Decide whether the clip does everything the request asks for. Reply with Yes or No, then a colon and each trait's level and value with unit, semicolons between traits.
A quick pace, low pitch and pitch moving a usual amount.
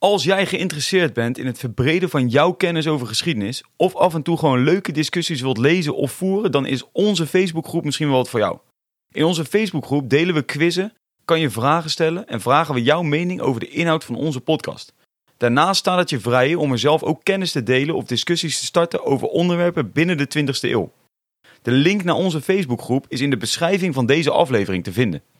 No: fast, 210 wpm; medium, 155 Hz; average, 4.7 semitones